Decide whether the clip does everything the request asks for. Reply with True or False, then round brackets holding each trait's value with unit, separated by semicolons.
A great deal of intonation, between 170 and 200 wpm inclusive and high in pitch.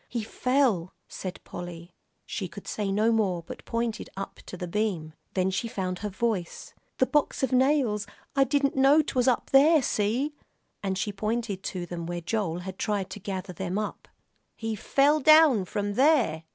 True (5.7 semitones; 180 wpm; 210 Hz)